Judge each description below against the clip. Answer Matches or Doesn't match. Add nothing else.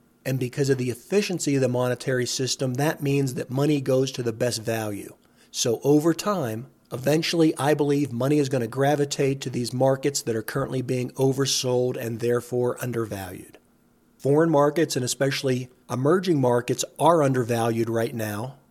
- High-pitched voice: Doesn't match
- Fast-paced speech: Doesn't match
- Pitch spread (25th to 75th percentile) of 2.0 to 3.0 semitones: Matches